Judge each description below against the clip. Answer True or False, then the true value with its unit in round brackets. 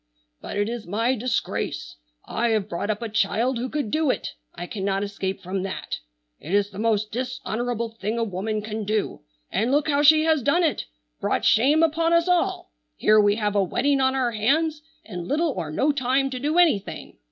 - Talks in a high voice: True (230 Hz)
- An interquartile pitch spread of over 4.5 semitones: True (5.5 semitones)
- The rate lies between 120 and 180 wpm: False (200 wpm)